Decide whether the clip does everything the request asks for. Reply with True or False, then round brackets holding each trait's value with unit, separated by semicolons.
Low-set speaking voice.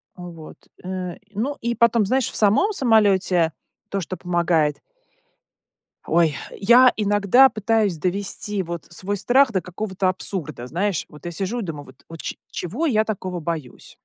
False (190 Hz)